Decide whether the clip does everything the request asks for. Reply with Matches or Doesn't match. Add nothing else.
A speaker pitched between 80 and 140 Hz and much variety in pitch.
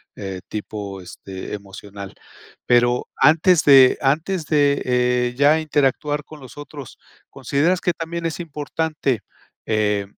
Matches